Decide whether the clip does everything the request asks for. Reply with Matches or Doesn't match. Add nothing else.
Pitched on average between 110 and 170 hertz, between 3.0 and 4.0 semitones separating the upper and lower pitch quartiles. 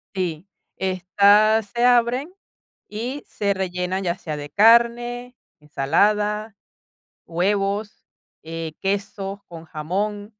Doesn't match